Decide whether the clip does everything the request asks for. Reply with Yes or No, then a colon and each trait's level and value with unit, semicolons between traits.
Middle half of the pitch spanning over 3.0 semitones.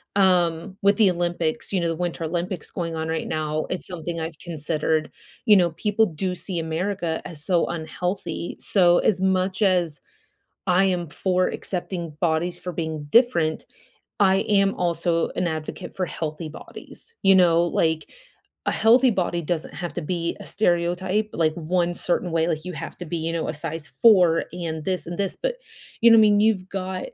No: narrow, 2.6 semitones